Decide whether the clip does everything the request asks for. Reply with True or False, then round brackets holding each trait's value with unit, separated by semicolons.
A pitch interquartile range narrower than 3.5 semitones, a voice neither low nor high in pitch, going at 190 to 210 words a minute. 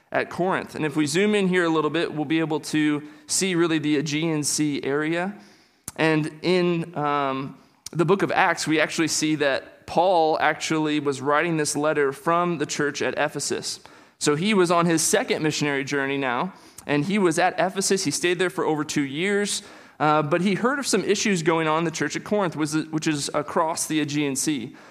True (2.8 semitones; 155 Hz; 200 wpm)